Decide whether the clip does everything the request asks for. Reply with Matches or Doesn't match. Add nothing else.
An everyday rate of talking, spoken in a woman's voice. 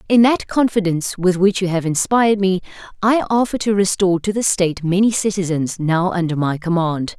Matches